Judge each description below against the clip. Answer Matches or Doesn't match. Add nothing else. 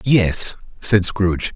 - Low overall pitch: Matches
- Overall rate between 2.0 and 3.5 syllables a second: Matches